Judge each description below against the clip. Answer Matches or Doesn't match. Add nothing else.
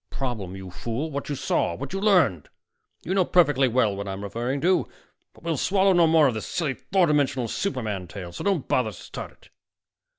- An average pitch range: Doesn't match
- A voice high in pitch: Doesn't match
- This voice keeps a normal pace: Doesn't match